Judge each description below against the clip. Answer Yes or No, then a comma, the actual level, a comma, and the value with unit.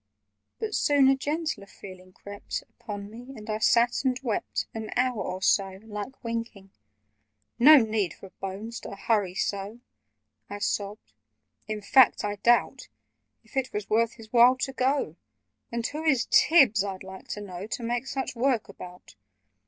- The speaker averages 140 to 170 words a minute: Yes, average, 160 wpm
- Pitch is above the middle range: Yes, high, 220 Hz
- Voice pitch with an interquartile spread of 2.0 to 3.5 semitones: No, average, 4.2 semitones